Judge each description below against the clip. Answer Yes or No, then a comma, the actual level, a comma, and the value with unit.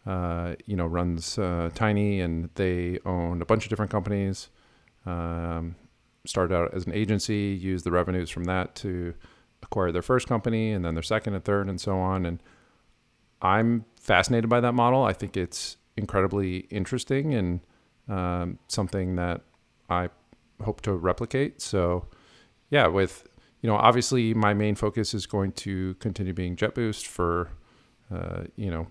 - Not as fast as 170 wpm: Yes, average, 160 wpm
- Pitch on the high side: No, very low, 95 Hz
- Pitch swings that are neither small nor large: Yes, average, 3.5 semitones